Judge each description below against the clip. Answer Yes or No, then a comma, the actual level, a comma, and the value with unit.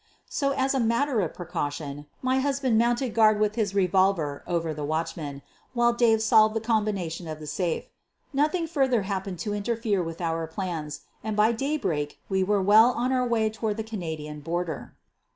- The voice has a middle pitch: No, high, 205 Hz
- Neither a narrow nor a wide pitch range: No, wide, 6.1 semitones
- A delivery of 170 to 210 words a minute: Yes, average, 185 wpm